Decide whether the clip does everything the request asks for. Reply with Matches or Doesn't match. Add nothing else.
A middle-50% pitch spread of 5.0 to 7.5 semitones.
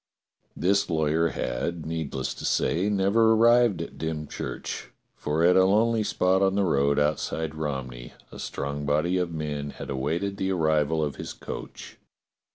Doesn't match